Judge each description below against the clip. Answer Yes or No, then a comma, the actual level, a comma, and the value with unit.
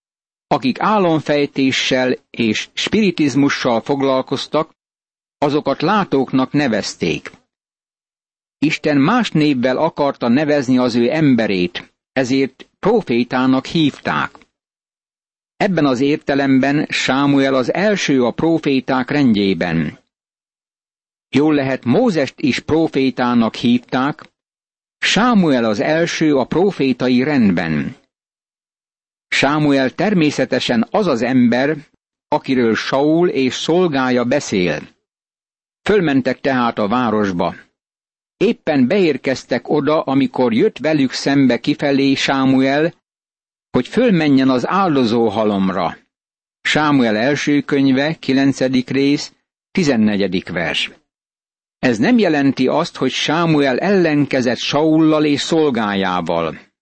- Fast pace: No, slow, 90 wpm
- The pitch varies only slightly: No, average, 3.2 semitones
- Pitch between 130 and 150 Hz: Yes, low, 135 Hz